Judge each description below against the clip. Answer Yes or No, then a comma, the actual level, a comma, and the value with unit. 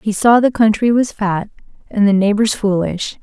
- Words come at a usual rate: Yes, average, 185 wpm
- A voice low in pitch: No, high, 210 Hz